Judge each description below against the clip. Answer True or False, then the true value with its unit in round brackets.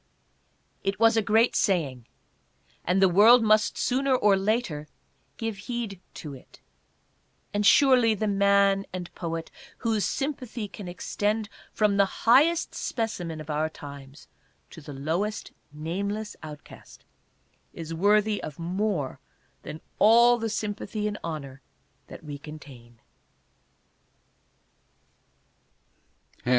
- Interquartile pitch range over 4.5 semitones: True (5.6 semitones)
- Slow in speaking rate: True (115 wpm)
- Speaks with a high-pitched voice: True (200 Hz)